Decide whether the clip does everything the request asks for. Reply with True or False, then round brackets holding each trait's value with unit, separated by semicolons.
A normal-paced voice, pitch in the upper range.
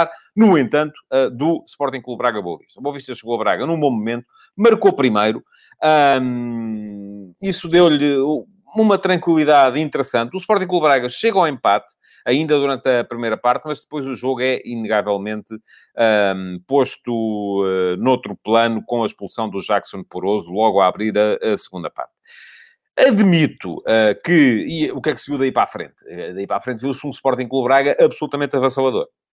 False (160 wpm; 130 Hz)